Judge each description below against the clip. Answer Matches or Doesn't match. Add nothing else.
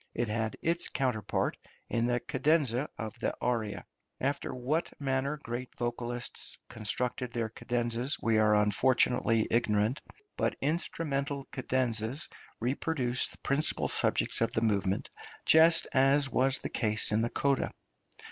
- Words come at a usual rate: Doesn't match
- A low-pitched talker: Matches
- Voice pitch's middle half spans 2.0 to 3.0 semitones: Doesn't match